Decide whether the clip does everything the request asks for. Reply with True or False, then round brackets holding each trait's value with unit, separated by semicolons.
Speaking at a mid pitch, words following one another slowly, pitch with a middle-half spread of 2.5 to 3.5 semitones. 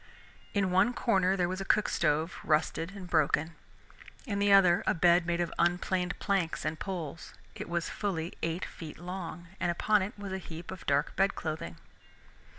False (175 Hz; 180 wpm; 2.8 semitones)